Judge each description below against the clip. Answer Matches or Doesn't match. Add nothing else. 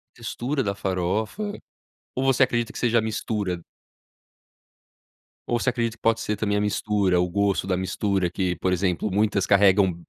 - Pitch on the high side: Doesn't match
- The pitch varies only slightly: Doesn't match